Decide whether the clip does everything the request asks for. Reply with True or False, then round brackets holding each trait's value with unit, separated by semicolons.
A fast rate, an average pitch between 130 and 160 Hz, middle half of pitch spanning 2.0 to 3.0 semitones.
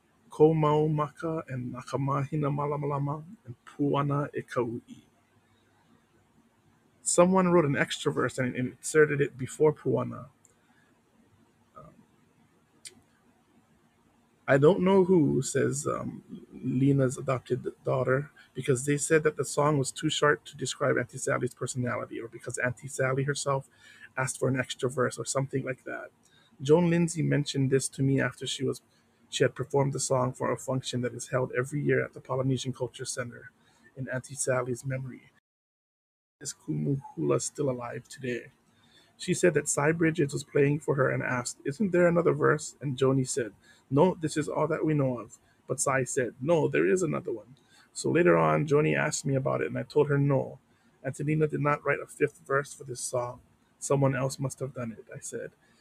False (165 wpm; 135 Hz; 2.7 semitones)